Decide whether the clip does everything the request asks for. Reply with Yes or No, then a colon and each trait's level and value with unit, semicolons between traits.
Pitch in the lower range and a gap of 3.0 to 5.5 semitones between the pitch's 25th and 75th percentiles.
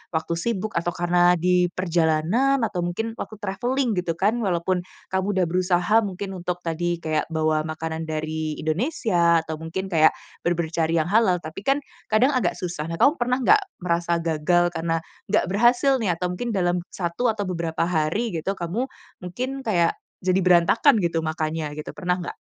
No: medium, 175 Hz; average, 3.9 semitones